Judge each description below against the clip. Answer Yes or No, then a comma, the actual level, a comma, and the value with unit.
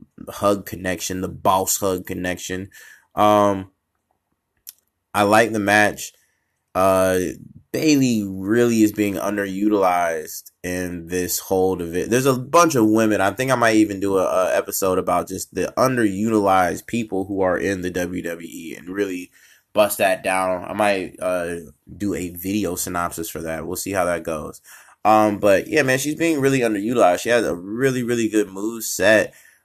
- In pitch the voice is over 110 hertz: No, low, 100 Hz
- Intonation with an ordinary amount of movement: Yes, average, 3.2 semitones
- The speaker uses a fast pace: No, average, 160 wpm